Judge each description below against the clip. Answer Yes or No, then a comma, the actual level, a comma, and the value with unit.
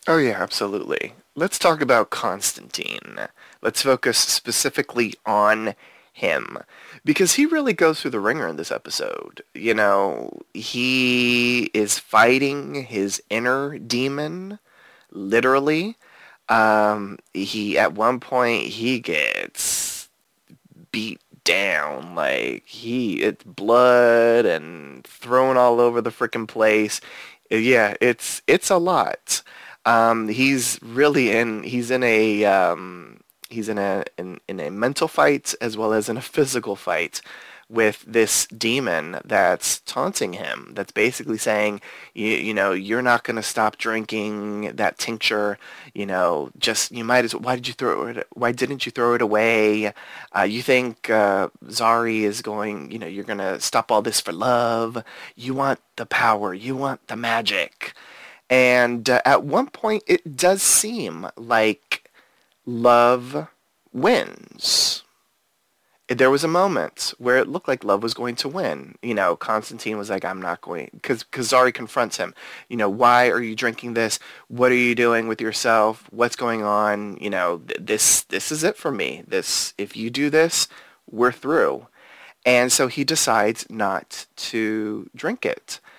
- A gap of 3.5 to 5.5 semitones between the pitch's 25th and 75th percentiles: No, average, 2.8 semitones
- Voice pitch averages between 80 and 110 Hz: No, low, 120 Hz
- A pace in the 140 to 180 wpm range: Yes, average, 150 wpm